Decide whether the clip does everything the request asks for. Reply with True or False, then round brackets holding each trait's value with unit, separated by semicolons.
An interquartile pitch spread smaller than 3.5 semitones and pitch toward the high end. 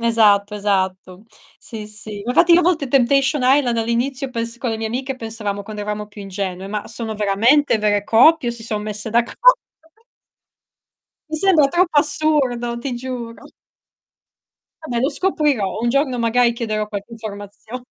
False (4.2 semitones; 235 Hz)